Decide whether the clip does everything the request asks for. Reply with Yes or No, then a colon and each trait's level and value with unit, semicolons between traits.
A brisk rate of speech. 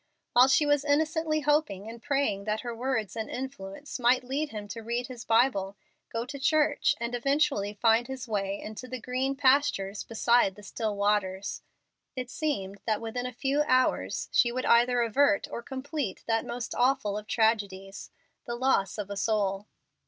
No: average, 175 wpm